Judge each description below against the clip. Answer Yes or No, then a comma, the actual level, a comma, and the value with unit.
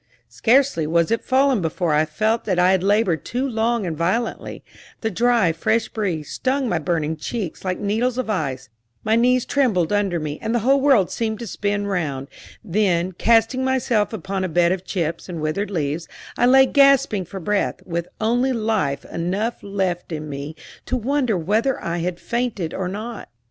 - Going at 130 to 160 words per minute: No, average, 180 wpm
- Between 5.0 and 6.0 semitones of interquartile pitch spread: Yes, wide, 5.6 semitones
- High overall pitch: Yes, high, 200 Hz